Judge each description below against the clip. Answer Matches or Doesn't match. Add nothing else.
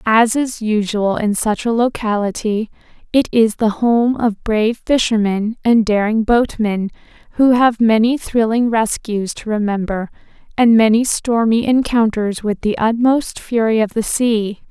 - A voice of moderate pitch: Doesn't match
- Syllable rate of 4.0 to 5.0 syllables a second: Matches